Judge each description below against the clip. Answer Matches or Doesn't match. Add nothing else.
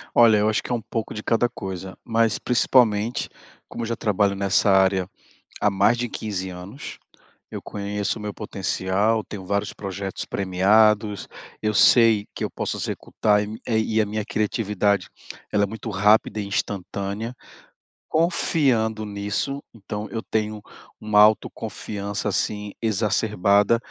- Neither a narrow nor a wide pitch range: Doesn't match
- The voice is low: Matches